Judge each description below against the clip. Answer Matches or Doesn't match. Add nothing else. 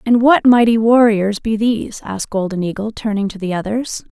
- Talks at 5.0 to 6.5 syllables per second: Matches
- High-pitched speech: Matches